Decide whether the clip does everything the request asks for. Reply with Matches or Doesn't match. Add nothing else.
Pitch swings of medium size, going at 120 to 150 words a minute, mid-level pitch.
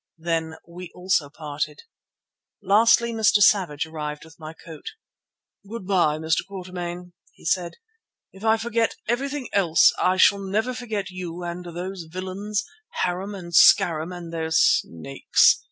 Matches